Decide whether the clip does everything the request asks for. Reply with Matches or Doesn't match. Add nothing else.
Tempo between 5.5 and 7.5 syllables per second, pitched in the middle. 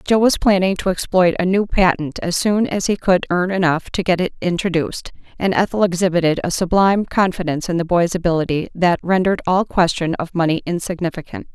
Matches